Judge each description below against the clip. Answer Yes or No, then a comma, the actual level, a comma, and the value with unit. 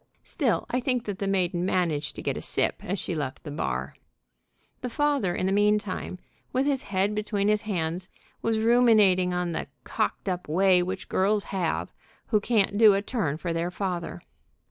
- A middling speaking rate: Yes, average, 190 wpm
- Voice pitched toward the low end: No, high, 195 Hz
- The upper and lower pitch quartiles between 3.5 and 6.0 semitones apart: No, average, 3.1 semitones